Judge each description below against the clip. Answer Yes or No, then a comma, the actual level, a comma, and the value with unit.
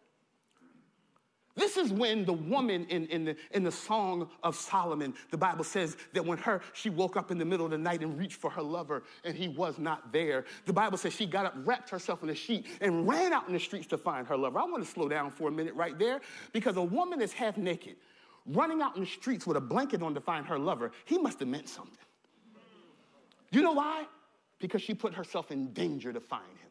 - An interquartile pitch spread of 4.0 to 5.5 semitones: Yes, average, 5.2 semitones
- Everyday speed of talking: No, fast, 235 wpm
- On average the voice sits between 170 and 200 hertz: Yes, medium, 185 Hz